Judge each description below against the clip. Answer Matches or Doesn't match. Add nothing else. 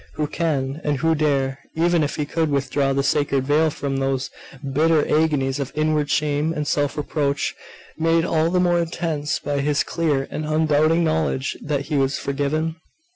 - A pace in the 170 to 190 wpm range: Matches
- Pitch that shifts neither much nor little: Doesn't match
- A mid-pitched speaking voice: Matches